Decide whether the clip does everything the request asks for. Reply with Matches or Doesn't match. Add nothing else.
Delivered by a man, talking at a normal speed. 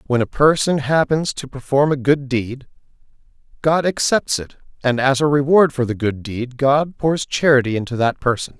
Matches